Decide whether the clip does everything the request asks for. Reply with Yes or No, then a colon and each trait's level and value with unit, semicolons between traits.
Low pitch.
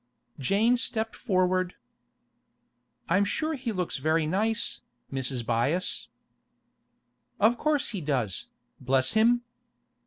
No: medium, 185 Hz